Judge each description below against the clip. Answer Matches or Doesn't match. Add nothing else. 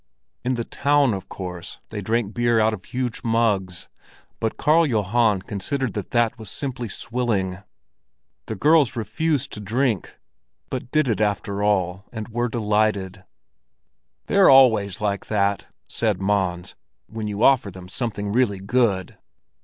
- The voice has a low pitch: Matches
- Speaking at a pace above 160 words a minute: Doesn't match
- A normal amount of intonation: Matches